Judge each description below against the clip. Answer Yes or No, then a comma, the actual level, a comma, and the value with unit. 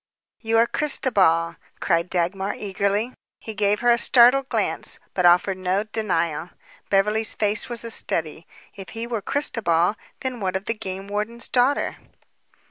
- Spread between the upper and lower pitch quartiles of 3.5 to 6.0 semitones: Yes, average, 3.8 semitones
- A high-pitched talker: Yes, high, 205 Hz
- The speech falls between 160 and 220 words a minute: No, average, 150 wpm